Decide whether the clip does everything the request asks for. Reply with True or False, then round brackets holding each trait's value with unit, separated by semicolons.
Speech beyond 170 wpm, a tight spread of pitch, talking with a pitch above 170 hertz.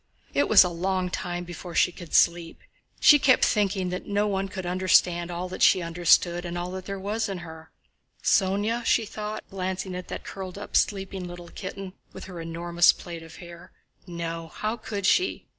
True (185 wpm; 2.3 semitones; 185 Hz)